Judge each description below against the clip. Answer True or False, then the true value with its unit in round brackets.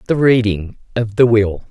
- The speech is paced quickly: False (175 wpm)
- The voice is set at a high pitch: False (110 Hz)